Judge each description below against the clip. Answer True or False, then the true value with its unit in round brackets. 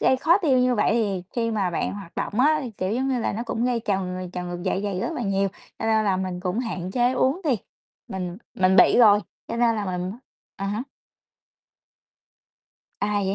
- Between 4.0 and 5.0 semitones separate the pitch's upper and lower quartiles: True (4.6 semitones)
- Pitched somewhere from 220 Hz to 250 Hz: False (205 Hz)